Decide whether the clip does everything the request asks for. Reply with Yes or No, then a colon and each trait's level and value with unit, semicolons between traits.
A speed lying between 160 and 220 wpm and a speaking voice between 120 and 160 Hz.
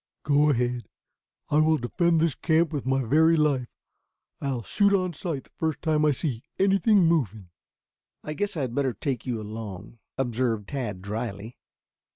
Yes: average, 165 wpm; medium, 140 Hz